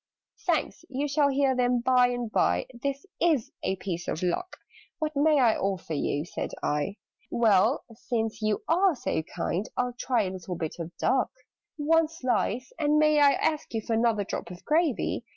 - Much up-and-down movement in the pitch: Yes, wide, 6.3 semitones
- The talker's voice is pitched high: Yes, high, 245 Hz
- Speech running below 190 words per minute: Yes, average, 180 wpm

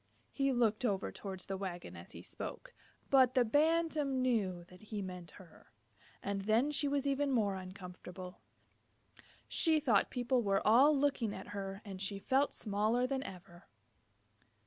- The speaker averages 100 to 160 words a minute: Yes, average, 155 wpm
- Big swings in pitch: Yes, wide, 6.0 semitones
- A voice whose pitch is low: No, high, 220 Hz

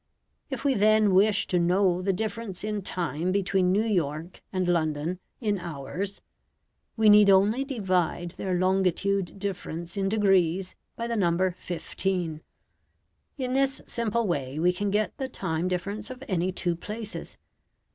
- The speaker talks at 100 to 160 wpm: Yes, average, 145 wpm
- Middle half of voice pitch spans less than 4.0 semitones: Yes, average, 3.1 semitones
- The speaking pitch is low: No, high, 190 Hz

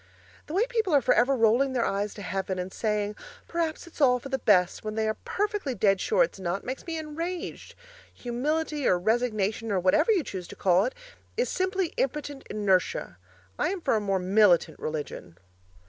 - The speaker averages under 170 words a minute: No, average, 190 wpm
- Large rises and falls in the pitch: Yes, wide, 8.0 semitones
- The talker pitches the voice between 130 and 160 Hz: No, high, 235 Hz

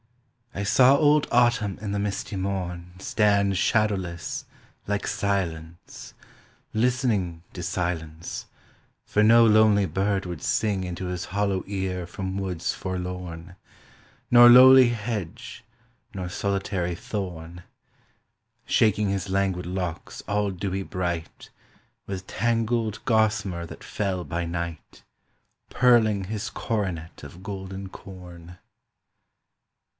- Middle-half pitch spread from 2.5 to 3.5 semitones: Yes, average, 3.0 semitones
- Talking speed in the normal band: No, slow, 110 wpm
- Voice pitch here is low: Yes, very low, 95 Hz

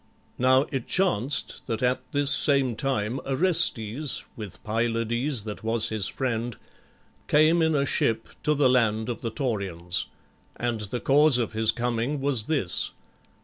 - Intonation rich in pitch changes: No, average, 3.9 semitones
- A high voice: No, low, 120 Hz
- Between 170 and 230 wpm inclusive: No, average, 145 wpm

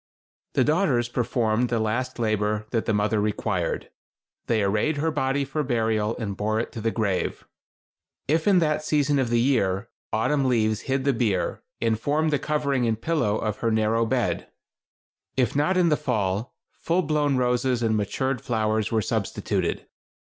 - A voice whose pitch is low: Yes, low, 120 Hz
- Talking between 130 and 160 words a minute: No, average, 170 wpm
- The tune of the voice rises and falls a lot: No, average, 4.6 semitones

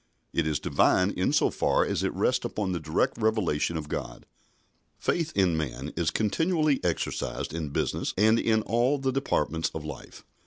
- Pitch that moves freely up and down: Yes, wide, 6.9 semitones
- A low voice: Yes, very low, 90 Hz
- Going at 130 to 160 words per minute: No, average, 170 wpm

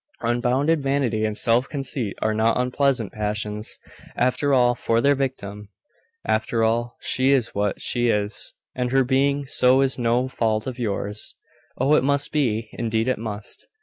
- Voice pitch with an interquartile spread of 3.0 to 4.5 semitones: Yes, average, 3.4 semitones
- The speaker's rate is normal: Yes, average, 160 wpm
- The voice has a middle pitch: No, low, 120 Hz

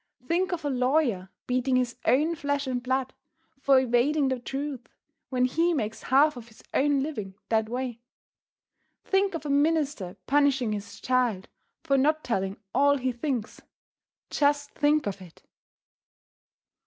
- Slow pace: No, average, 145 wpm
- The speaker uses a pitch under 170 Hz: No, very high, 265 Hz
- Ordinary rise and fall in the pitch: Yes, average, 3.3 semitones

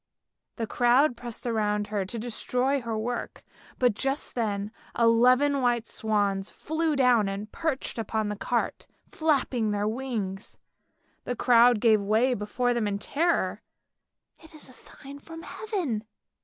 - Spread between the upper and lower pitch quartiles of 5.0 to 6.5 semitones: No, average, 3.9 semitones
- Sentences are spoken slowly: No, average, 145 wpm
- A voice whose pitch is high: Yes, high, 240 Hz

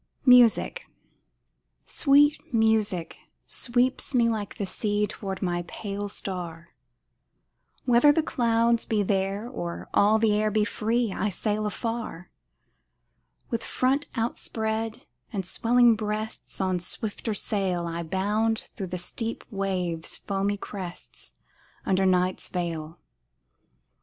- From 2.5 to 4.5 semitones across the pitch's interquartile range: Yes, average, 3.4 semitones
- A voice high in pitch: Yes, high, 210 Hz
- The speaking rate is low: Yes, slow, 115 wpm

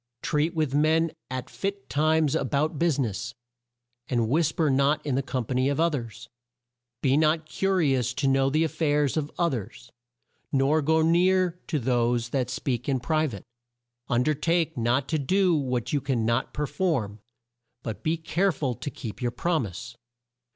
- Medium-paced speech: Yes, average, 195 wpm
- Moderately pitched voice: Yes, medium, 145 Hz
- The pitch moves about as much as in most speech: Yes, average, 4.1 semitones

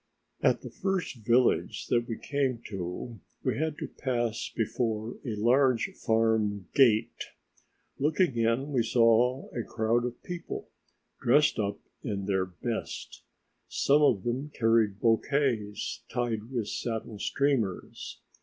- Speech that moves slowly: Yes, slow, 125 wpm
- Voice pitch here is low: Yes, low, 115 Hz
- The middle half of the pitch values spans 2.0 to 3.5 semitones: Yes, average, 3.2 semitones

